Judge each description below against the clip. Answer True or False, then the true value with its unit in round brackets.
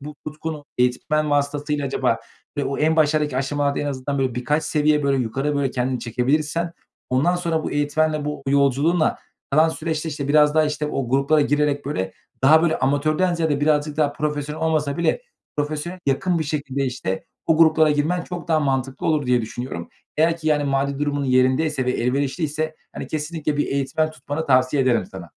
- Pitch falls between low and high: True (145 Hz)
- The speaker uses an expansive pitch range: False (2.4 semitones)